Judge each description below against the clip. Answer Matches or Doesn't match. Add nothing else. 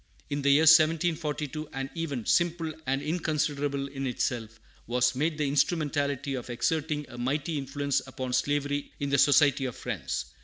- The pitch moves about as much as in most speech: Doesn't match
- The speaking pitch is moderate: Matches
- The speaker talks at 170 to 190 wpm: Doesn't match